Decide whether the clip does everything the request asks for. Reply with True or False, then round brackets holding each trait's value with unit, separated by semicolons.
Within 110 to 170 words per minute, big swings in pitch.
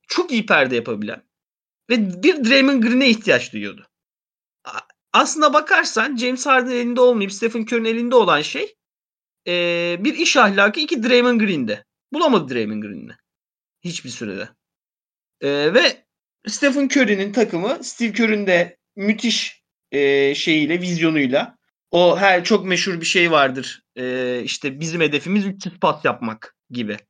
True (125 wpm; 7.1 semitones)